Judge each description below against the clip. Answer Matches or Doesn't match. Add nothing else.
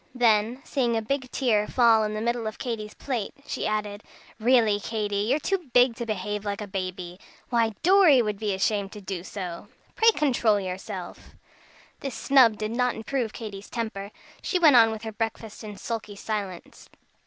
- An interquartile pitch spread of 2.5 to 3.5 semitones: Matches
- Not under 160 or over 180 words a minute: Matches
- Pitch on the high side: Matches